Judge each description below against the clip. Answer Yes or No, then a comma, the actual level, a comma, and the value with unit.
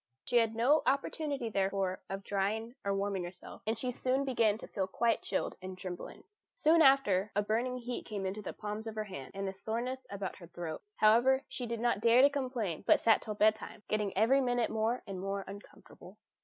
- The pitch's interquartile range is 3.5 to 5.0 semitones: Yes, average, 3.8 semitones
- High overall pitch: Yes, high, 220 Hz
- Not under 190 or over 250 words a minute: Yes, fast, 205 wpm